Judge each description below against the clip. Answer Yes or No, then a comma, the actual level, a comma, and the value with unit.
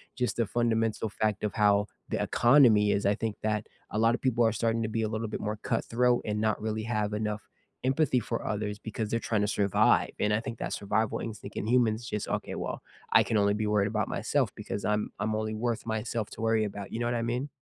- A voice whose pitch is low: Yes, low, 110 Hz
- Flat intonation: Yes, narrow, 1.7 semitones